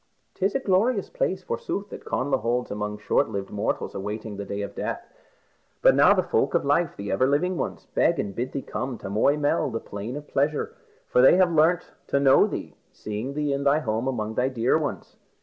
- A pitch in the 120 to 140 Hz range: Yes, low, 135 Hz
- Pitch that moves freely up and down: Yes, wide, 6.3 semitones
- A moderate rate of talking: No, fast, 215 wpm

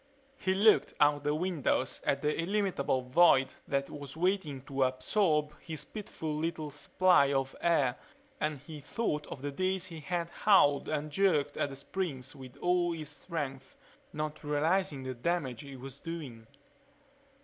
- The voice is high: No, medium, 150 Hz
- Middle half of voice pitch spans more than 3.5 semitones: Yes, average, 4.0 semitones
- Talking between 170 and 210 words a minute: No, average, 155 wpm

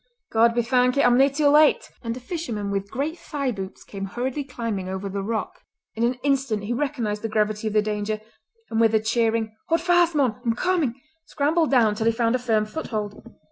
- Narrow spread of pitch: No, average, 4.3 semitones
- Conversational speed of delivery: No, fast, 210 wpm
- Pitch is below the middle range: No, high, 230 Hz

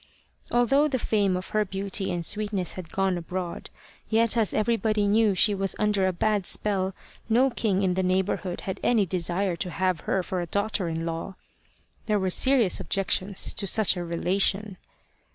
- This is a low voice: No, high, 195 Hz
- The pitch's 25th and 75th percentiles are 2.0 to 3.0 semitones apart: Yes, narrow, 2.6 semitones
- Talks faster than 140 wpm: Yes, average, 175 wpm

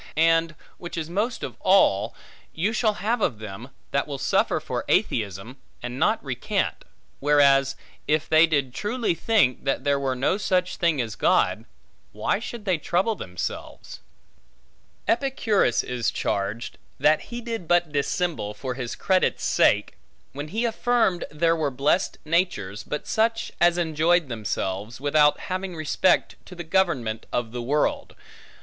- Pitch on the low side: No, medium, 155 Hz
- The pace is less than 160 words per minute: Yes, average, 150 wpm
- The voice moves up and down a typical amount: No, wide, 6.5 semitones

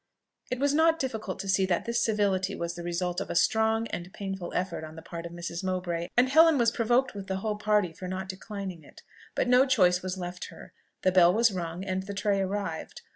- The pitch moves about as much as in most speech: Yes, average, 3.8 semitones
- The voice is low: No, high, 190 Hz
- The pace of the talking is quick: Yes, fast, 230 wpm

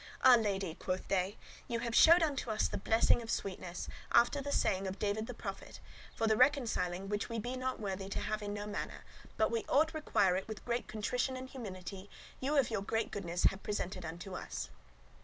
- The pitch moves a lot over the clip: No, average, 4.1 semitones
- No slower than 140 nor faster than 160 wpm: No, fast, 205 wpm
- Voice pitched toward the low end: No, high, 215 Hz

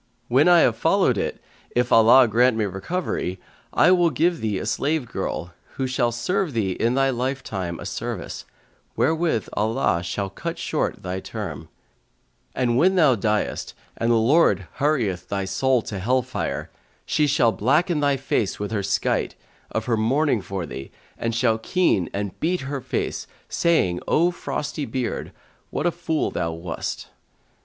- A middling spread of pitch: No, wide, 6.4 semitones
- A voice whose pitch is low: Yes, low, 120 Hz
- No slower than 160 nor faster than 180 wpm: Yes, average, 165 wpm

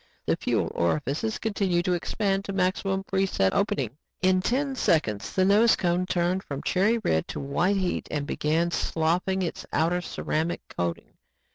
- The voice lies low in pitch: No, medium, 180 Hz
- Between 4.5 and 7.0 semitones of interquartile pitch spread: No, average, 3.8 semitones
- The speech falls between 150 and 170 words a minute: Yes, average, 160 wpm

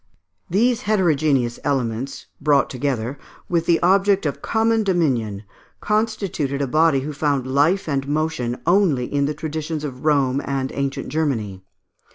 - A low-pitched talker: No, medium, 145 Hz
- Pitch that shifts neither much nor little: Yes, average, 4.1 semitones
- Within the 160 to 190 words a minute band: No, average, 140 wpm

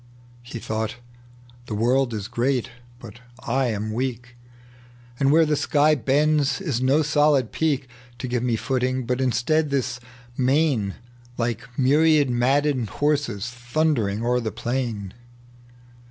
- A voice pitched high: No, low, 125 Hz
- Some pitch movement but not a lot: Yes, average, 3.4 semitones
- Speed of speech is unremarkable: No, slow, 130 wpm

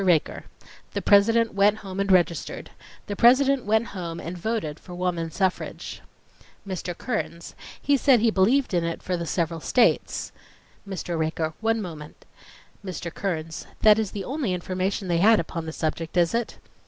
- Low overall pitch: No, medium, 185 Hz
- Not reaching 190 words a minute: Yes, average, 165 wpm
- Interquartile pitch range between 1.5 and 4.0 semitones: No, average, 4.6 semitones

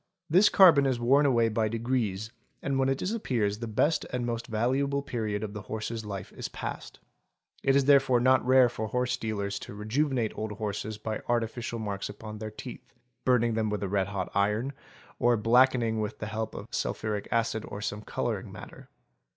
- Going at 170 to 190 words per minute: Yes, average, 185 wpm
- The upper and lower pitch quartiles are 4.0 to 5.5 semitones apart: No, average, 3.2 semitones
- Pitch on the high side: No, low, 115 Hz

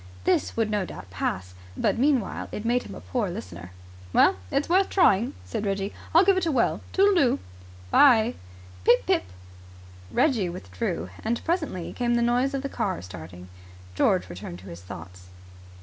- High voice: Yes, high, 215 Hz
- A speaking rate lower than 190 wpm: Yes, average, 170 wpm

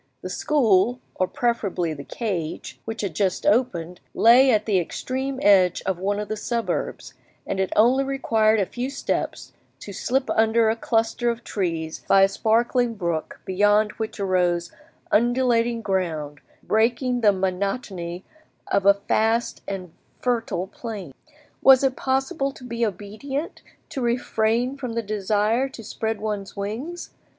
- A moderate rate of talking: Yes, average, 145 wpm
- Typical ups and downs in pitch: Yes, average, 3.9 semitones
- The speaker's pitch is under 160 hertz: No, high, 220 Hz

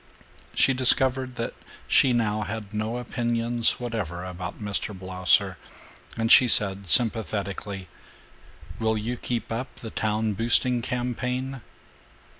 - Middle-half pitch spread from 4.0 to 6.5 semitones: No, average, 2.9 semitones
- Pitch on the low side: Yes, low, 115 Hz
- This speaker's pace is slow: Yes, slow, 115 wpm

